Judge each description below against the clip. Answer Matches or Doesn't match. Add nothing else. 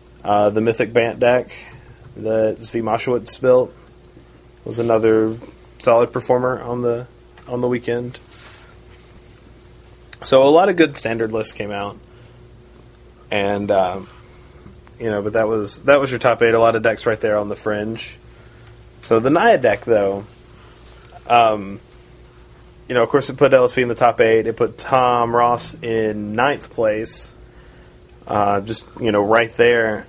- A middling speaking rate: Matches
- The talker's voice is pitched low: Matches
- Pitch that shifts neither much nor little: Doesn't match